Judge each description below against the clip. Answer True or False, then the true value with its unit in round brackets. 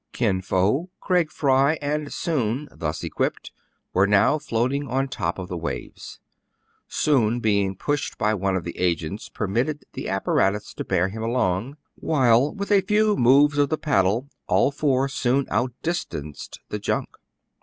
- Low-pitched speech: True (125 Hz)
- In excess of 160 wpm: False (155 wpm)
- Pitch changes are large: True (6.9 semitones)